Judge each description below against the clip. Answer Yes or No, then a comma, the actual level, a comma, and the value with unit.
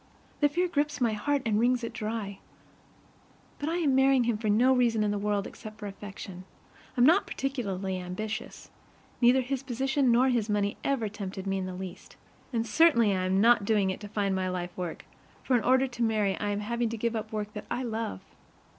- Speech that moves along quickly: Yes, fast, 210 wpm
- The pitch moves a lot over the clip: No, average, 3.8 semitones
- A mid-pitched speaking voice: No, high, 220 Hz